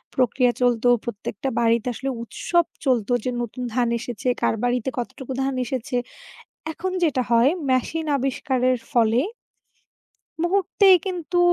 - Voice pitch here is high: Yes, very high, 255 Hz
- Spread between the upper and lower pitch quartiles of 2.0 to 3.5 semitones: Yes, average, 3.1 semitones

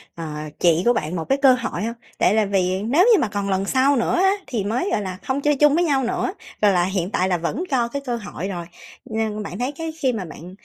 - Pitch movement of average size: No, wide, 6.3 semitones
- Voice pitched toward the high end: Yes, high, 220 Hz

